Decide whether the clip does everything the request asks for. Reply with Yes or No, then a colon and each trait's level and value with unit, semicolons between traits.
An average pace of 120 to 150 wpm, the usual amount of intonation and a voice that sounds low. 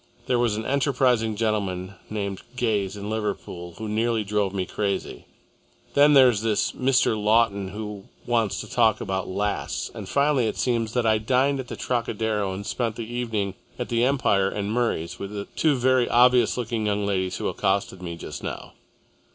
No: average, 175 wpm; average, 3.3 semitones; low, 110 Hz